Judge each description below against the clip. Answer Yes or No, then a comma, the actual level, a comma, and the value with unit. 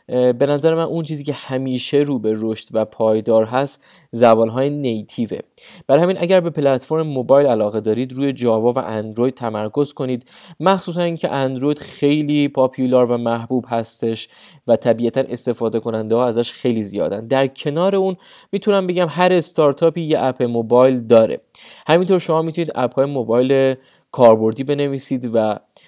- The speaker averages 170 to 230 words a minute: No, average, 155 wpm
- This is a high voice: No, low, 130 Hz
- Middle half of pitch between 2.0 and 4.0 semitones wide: No, average, 4.8 semitones